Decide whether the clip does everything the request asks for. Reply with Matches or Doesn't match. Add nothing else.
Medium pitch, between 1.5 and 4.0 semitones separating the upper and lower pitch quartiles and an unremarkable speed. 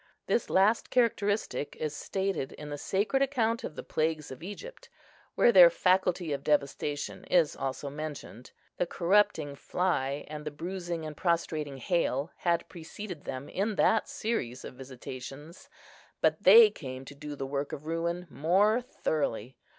Doesn't match